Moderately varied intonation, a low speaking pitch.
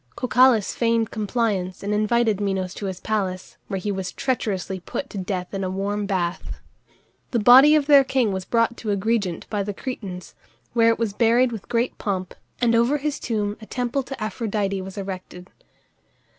No: average, 3.6 semitones; high, 210 Hz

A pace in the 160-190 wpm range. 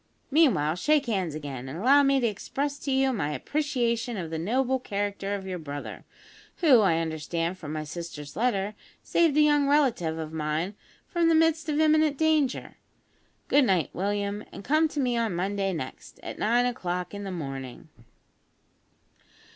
Yes: average, 170 wpm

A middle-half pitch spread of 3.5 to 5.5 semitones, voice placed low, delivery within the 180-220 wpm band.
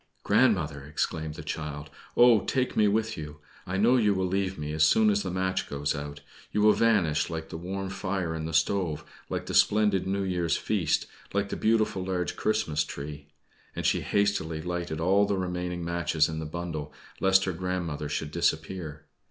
Yes: average, 4.0 semitones; very low, 90 Hz; average, 185 wpm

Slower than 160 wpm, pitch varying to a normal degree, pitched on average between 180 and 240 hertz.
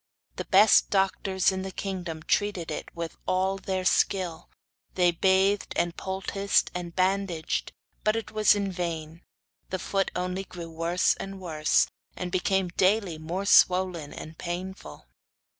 No: average, 140 wpm; narrow, 2.2 semitones; medium, 185 Hz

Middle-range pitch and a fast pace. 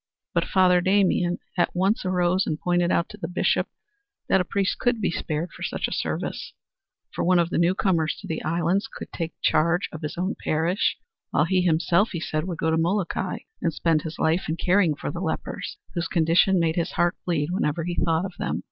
Yes: medium, 175 Hz; fast, 210 wpm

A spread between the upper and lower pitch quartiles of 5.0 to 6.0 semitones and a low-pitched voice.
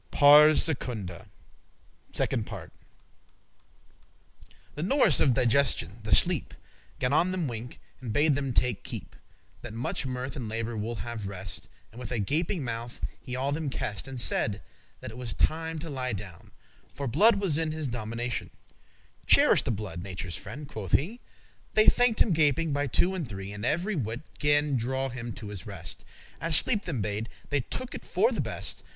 Yes: wide, 5.6 semitones; low, 130 Hz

